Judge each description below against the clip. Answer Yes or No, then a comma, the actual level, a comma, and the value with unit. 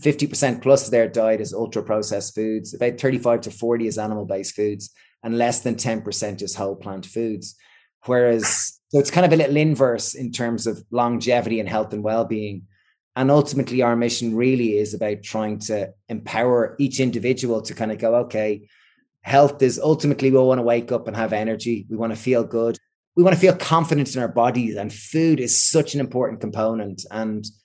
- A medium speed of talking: Yes, average, 195 wpm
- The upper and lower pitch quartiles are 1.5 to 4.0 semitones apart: Yes, average, 3.1 semitones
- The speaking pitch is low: Yes, low, 115 Hz